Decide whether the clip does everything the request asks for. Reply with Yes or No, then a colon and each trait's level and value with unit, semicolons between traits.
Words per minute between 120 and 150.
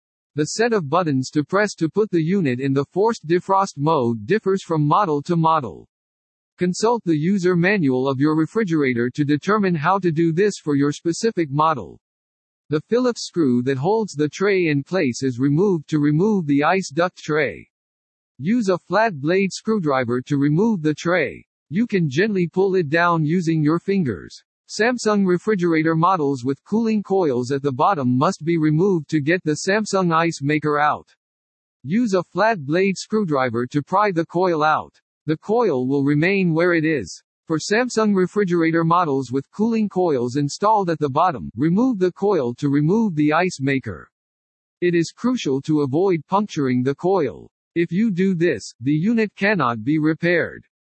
No: average, 170 wpm